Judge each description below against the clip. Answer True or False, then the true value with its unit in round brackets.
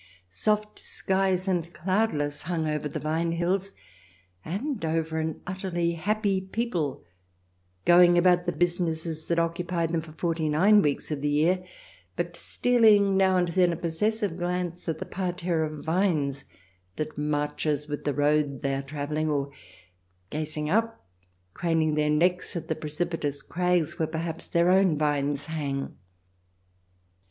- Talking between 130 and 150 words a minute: True (145 wpm)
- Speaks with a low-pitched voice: False (165 Hz)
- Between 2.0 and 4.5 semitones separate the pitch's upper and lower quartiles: True (3.1 semitones)